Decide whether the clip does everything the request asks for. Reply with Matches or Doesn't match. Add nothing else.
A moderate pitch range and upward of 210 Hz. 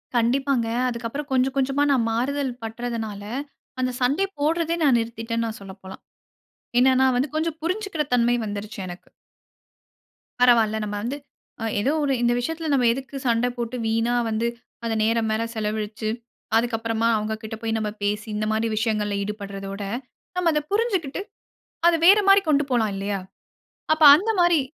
Matches